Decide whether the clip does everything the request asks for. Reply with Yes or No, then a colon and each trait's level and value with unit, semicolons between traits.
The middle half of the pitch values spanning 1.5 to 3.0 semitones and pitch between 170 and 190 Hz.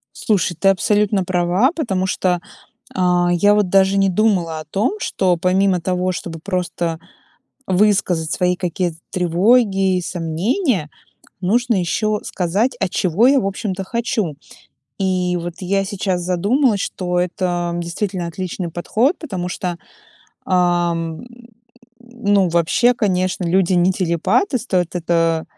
Yes: narrow, 2.6 semitones; medium, 185 Hz